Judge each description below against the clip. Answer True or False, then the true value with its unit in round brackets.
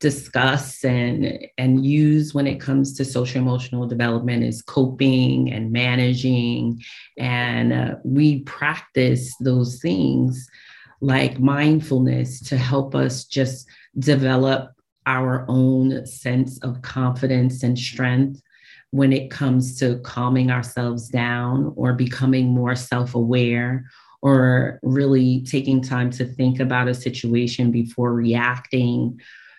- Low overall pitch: True (130 Hz)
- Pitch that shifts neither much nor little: False (1.4 semitones)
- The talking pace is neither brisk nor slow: False (115 wpm)